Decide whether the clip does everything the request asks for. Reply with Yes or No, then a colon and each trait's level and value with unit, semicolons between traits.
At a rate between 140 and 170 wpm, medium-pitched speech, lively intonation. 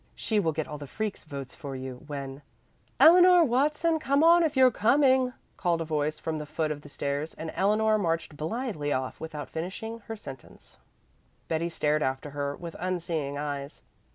No: average, 180 wpm; medium, 160 Hz; wide, 7.3 semitones